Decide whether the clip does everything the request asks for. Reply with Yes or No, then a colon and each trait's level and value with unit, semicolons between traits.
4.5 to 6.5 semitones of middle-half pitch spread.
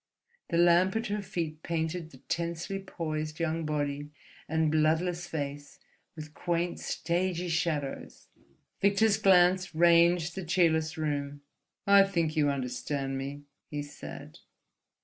No: average, 2.7 semitones